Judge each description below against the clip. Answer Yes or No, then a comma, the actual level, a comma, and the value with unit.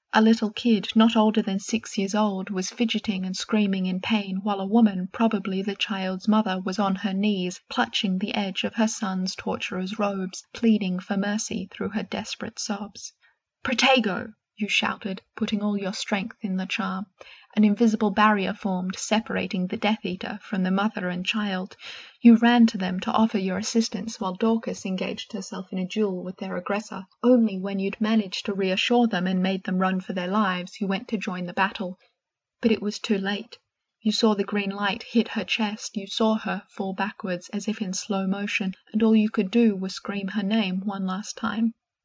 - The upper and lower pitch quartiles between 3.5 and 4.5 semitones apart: No, narrow, 2.4 semitones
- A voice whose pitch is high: Yes, high, 205 Hz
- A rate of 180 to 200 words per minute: Yes, average, 195 wpm